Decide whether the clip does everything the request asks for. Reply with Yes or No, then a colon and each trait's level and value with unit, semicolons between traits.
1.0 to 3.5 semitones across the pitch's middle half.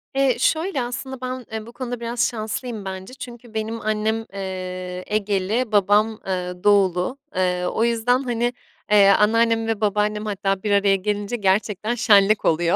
Yes: average, 3.2 semitones